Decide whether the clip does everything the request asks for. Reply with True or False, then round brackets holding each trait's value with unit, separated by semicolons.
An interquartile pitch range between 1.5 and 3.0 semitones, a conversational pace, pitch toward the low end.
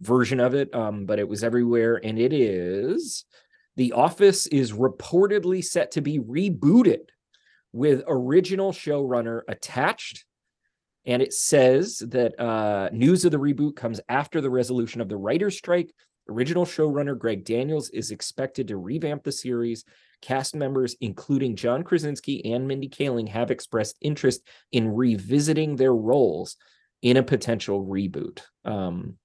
False (4.5 semitones; 145 wpm; 130 Hz)